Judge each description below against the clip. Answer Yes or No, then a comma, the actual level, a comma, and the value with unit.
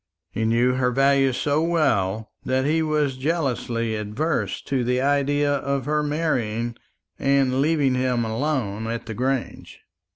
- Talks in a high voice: No, low, 130 Hz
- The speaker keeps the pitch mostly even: No, average, 3.6 semitones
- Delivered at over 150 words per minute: No, average, 140 wpm